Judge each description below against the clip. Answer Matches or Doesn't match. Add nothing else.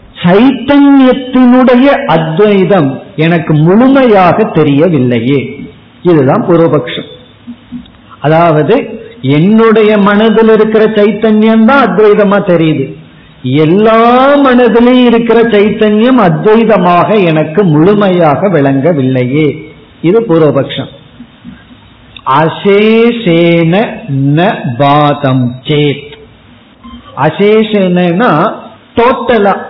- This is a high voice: Matches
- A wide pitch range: Matches